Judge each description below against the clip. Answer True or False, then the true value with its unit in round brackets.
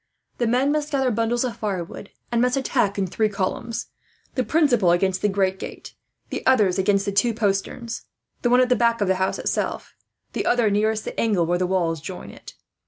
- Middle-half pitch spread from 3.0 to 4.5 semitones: True (4.1 semitones)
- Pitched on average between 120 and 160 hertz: False (215 Hz)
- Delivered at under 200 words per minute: False (205 wpm)